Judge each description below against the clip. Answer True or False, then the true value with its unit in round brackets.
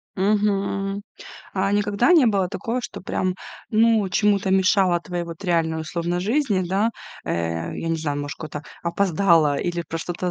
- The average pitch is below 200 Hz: True (185 Hz)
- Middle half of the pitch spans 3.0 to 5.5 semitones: True (3.5 semitones)